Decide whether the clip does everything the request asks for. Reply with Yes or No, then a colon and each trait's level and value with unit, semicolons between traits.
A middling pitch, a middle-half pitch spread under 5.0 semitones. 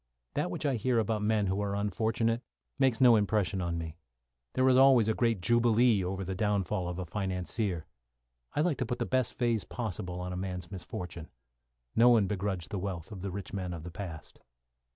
No: low, 100 Hz; average, 4.1 semitones